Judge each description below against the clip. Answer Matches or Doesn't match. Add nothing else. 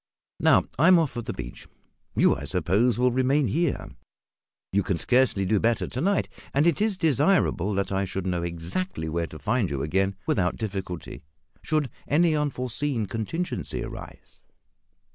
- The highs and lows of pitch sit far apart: Matches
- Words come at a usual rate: Matches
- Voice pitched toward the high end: Doesn't match